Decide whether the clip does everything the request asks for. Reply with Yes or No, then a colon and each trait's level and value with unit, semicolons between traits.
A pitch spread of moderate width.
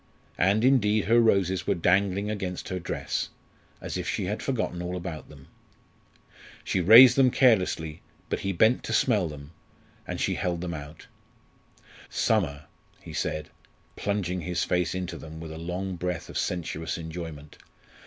Yes: average, 3.8 semitones